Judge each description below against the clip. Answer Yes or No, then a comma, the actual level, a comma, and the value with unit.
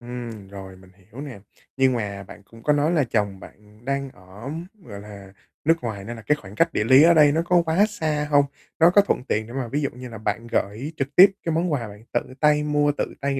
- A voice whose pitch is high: No, low, 125 Hz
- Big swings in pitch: Yes, wide, 6.1 semitones